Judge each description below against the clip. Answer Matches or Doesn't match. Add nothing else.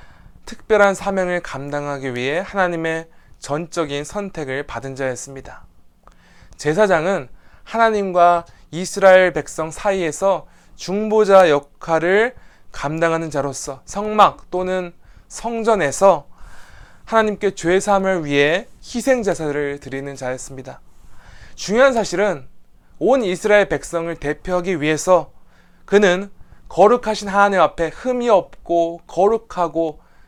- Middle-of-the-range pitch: Matches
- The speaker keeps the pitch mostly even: Doesn't match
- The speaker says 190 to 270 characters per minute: Matches